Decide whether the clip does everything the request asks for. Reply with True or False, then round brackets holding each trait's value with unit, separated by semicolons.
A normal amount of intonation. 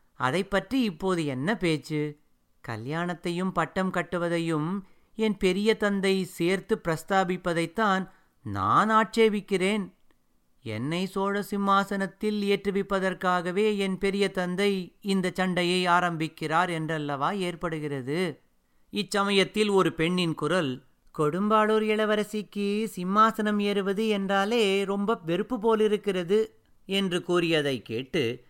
True (3.6 semitones)